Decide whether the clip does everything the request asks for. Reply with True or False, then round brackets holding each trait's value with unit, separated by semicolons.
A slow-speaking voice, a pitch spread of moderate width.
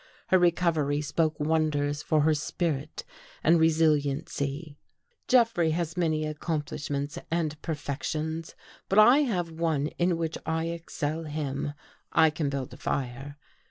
False (130 wpm; 2.3 semitones)